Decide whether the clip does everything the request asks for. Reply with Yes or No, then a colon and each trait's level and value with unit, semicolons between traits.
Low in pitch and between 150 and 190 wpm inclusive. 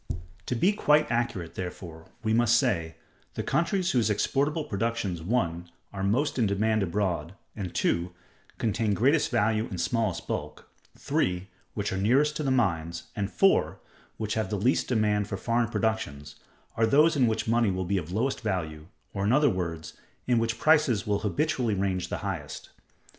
Yes: low, 110 Hz; average, 170 wpm